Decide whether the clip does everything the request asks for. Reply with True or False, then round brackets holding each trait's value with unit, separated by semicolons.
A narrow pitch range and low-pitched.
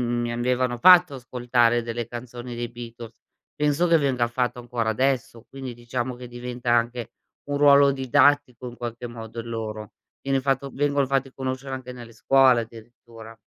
True (2.2 semitones; 120 Hz)